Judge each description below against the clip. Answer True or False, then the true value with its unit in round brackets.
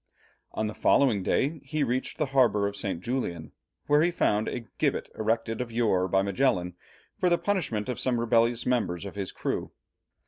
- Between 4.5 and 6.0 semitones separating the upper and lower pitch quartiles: True (4.8 semitones)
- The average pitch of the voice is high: False (115 Hz)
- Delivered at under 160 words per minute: False (180 wpm)